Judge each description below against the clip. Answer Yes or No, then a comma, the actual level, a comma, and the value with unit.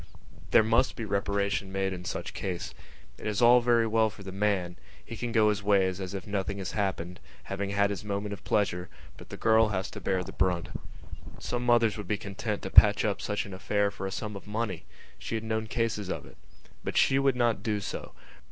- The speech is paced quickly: Yes, fast, 220 wpm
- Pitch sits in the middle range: No, low, 100 Hz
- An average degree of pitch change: No, narrow, 2.3 semitones